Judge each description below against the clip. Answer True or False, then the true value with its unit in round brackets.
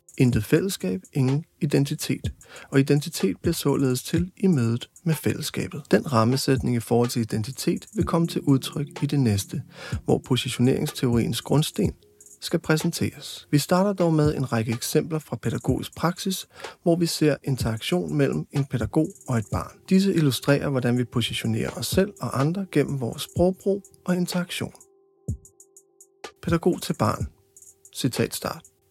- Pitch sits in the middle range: True (145 Hz)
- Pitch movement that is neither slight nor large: False (6.1 semitones)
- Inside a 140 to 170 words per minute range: True (145 wpm)